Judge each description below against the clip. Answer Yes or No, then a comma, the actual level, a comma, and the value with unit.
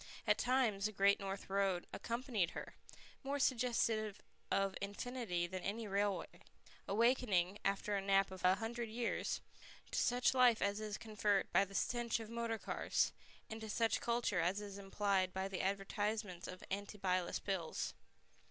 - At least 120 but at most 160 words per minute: Yes, average, 155 wpm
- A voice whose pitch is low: No, high, 205 Hz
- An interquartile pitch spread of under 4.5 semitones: Yes, average, 2.9 semitones